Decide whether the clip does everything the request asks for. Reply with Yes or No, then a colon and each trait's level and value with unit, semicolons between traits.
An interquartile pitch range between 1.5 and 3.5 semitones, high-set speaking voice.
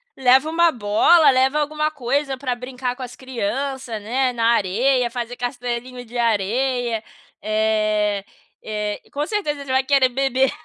Yes: average, 2.8 semitones; very high, 250 Hz